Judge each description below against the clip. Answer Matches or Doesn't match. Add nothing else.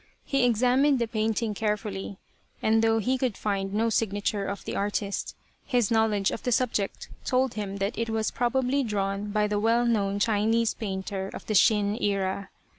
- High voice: Matches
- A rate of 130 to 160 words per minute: Doesn't match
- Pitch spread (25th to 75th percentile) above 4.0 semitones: Doesn't match